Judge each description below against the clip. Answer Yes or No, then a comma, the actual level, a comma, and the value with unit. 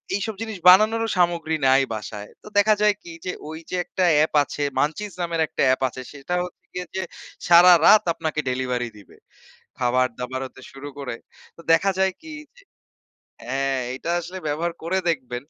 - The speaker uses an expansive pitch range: Yes, wide, 6.2 semitones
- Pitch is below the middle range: No, medium, 160 Hz